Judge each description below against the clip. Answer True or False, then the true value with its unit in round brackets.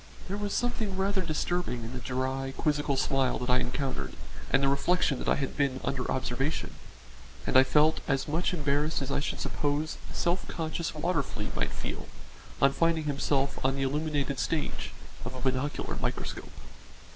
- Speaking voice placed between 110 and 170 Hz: True (140 Hz)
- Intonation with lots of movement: False (3.1 semitones)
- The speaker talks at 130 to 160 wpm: False (175 wpm)